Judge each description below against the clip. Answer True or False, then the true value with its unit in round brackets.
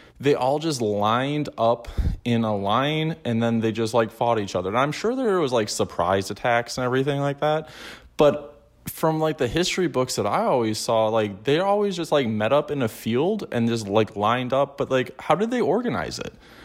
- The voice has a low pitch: True (125 Hz)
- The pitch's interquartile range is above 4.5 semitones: True (4.9 semitones)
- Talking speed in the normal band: False (215 wpm)